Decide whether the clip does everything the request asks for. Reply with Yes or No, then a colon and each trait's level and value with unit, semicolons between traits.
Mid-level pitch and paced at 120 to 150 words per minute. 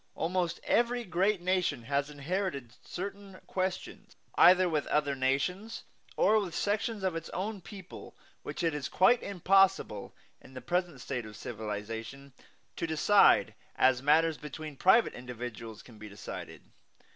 Yes: medium, 165 Hz; average, 140 wpm